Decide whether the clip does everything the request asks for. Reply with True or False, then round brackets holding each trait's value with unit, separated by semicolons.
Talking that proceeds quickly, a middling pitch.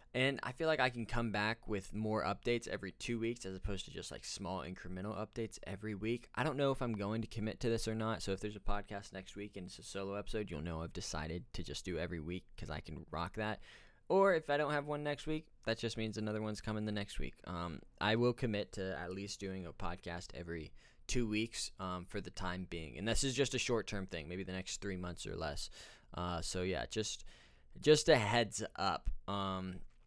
False (240 wpm; 105 Hz)